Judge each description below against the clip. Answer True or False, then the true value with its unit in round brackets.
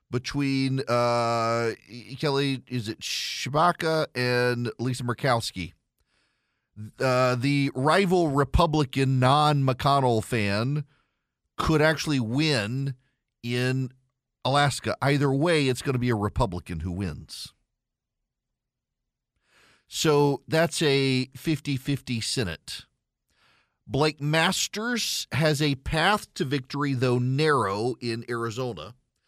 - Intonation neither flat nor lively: True (3.3 semitones)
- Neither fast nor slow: False (100 wpm)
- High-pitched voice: False (130 Hz)